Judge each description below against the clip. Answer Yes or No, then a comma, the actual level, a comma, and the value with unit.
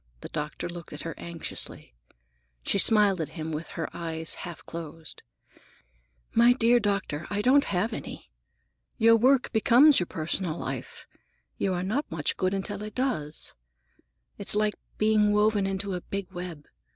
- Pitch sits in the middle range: No, high, 195 Hz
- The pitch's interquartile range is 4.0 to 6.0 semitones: Yes, average, 4.6 semitones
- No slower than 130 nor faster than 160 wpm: Yes, average, 155 wpm